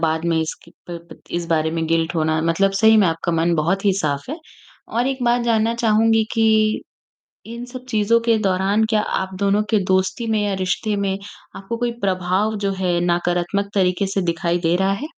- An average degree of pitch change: Yes, average, 4.1 semitones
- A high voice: Yes, high, 195 Hz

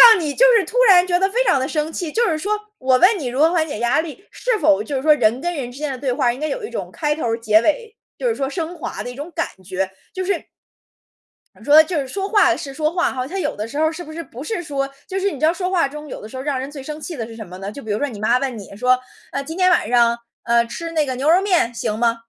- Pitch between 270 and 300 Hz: Yes, very high, 295 Hz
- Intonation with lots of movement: Yes, wide, 6.0 semitones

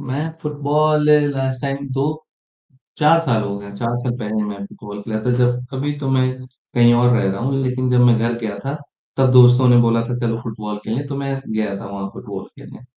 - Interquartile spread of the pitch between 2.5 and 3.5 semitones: Yes, average, 3.2 semitones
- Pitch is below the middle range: Yes, low, 125 Hz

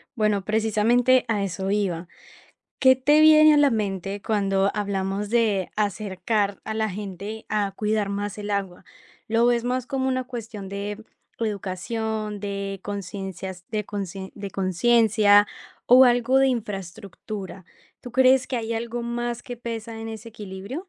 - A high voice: Yes, high, 210 Hz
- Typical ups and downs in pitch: Yes, average, 3.1 semitones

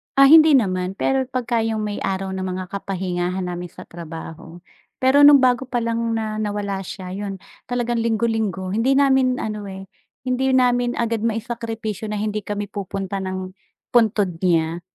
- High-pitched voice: Yes, high, 210 Hz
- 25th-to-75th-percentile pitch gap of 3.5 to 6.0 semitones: Yes, average, 4.3 semitones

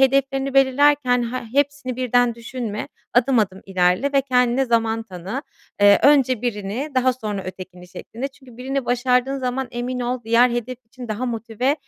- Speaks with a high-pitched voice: Yes, very high, 250 Hz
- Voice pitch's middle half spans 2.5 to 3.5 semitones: Yes, average, 2.8 semitones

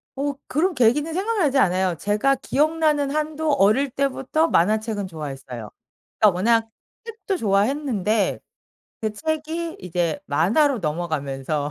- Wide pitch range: Yes, wide, 8.8 semitones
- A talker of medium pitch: No, high, 230 Hz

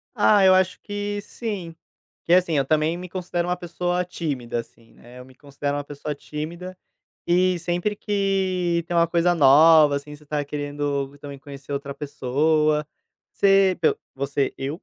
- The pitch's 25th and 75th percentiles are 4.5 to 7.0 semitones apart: No, average, 4.1 semitones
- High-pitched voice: No, medium, 160 Hz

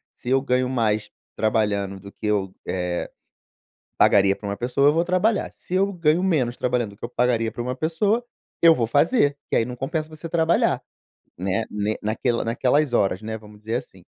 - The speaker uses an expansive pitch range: Yes, wide, 6.5 semitones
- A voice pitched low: Yes, low, 120 Hz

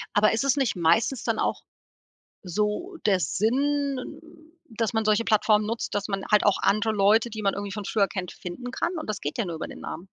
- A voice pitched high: Yes, high, 215 Hz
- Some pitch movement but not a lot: Yes, average, 3.0 semitones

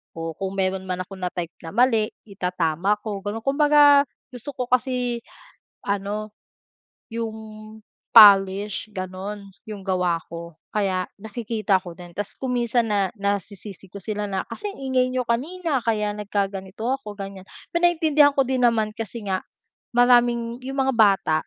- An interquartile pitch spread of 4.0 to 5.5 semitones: Yes, average, 4.3 semitones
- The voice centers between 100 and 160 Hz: No, high, 210 Hz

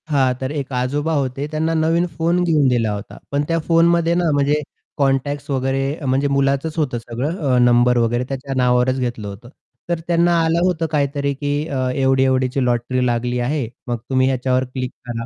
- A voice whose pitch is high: No, low, 135 Hz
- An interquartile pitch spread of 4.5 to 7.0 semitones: No, average, 3.3 semitones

